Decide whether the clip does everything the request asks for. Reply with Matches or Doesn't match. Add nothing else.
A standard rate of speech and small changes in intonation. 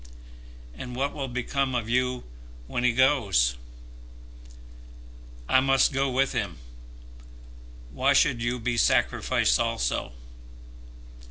Doesn't match